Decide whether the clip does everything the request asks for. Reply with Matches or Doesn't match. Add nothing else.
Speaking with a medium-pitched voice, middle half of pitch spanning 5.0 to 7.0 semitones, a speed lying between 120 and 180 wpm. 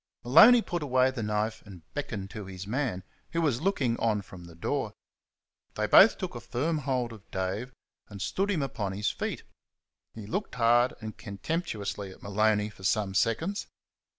Doesn't match